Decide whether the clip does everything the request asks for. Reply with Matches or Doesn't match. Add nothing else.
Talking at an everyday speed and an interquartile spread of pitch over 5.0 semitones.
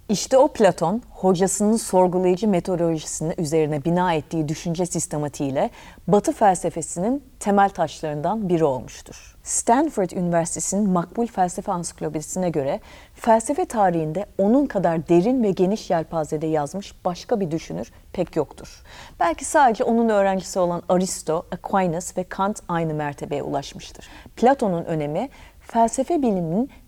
Doesn't match